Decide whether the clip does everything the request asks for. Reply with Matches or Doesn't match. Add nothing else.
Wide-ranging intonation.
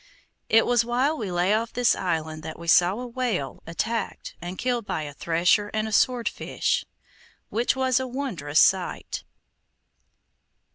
Matches